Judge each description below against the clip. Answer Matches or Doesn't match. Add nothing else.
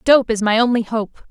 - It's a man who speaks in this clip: Doesn't match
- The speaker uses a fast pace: Matches